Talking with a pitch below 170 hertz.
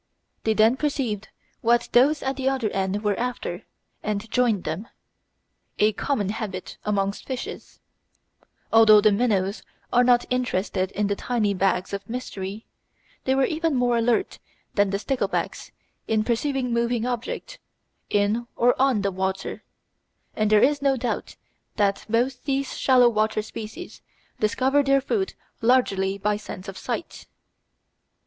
No: high, 225 Hz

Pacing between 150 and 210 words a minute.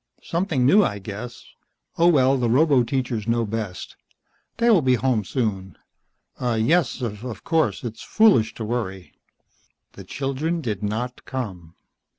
No: slow, 135 wpm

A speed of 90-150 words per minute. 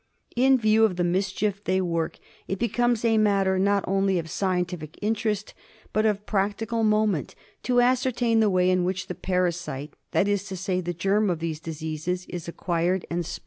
No: average, 185 wpm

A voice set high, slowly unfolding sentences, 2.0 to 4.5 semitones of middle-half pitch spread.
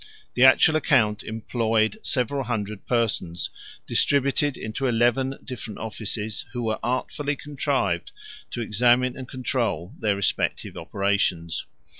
No: low, 115 Hz; slow, 115 wpm; average, 3.7 semitones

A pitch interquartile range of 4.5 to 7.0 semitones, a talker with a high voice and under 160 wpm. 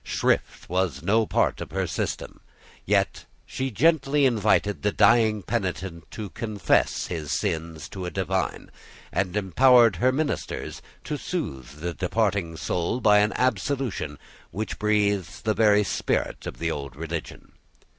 No: average, 5.2 semitones; low, 100 Hz; average, 140 wpm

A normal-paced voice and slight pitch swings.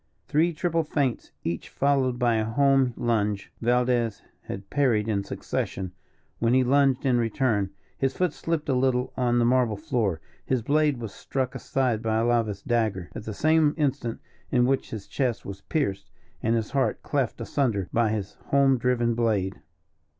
No: average, 165 wpm; average, 3.6 semitones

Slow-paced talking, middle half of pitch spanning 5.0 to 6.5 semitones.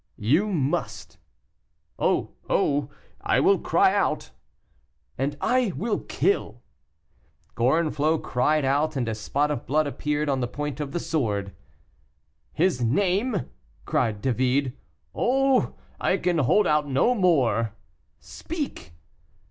Yes: slow, 120 wpm; wide, 5.5 semitones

